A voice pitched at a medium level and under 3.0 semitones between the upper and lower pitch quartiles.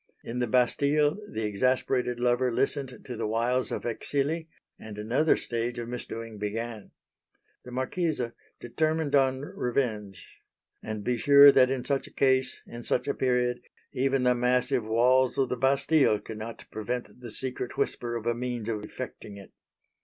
No: low, 125 Hz; narrow, 2.5 semitones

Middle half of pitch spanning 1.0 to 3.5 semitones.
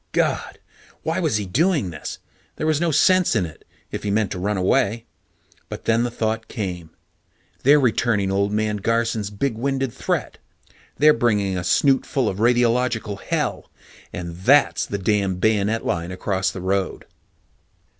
No: average, 4.0 semitones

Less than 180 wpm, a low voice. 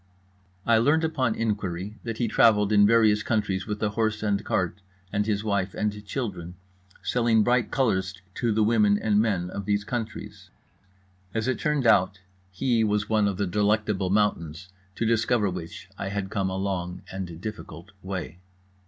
Yes: average, 170 wpm; low, 105 Hz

